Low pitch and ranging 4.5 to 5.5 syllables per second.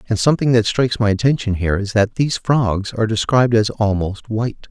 No: low, 110 Hz; 6.2 syllables/s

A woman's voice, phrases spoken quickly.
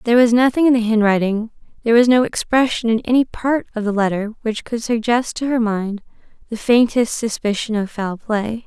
No: female; average, 195 wpm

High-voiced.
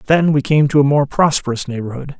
No: medium, 140 Hz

